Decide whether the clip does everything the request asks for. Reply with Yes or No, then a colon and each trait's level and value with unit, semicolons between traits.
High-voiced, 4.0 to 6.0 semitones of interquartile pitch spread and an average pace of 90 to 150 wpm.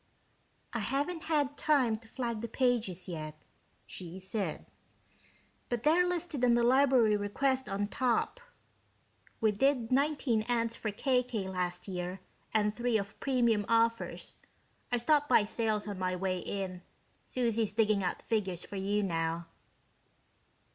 Yes: high, 225 Hz; average, 4.5 semitones; average, 140 wpm